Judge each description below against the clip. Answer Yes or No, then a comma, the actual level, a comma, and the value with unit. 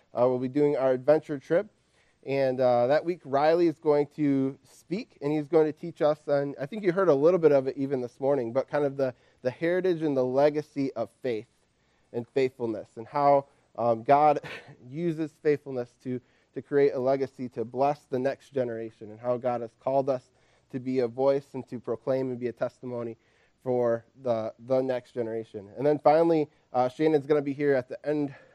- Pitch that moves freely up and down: No, average, 3.0 semitones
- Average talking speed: No, fast, 210 wpm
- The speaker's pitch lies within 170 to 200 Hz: No, low, 135 Hz